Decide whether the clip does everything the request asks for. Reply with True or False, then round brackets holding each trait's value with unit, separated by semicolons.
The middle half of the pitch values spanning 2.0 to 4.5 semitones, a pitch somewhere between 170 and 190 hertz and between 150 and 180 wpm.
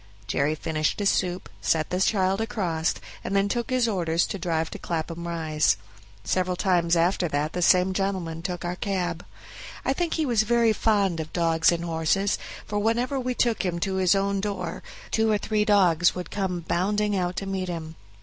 False (3.5 semitones; 185 Hz; 190 wpm)